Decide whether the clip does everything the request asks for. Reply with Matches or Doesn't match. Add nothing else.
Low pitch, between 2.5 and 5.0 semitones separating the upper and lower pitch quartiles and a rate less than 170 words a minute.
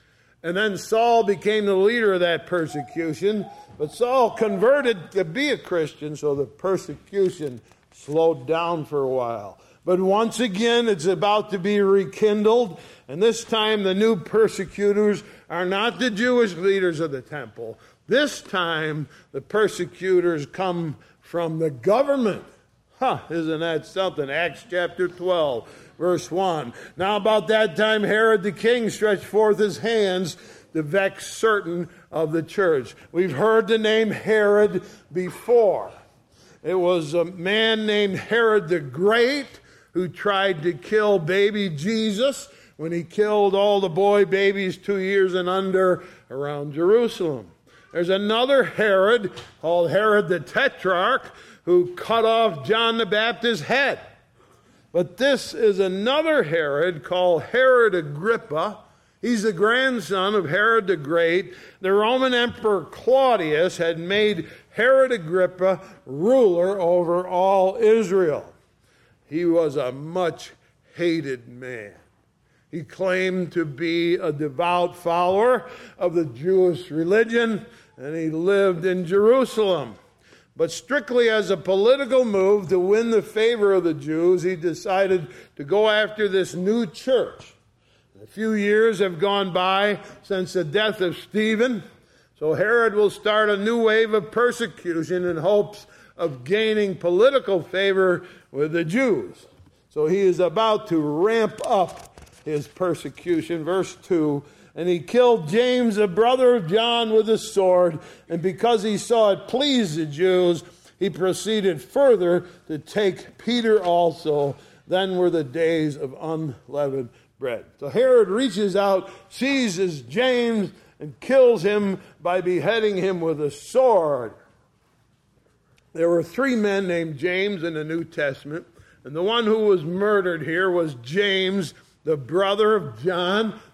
Doesn't match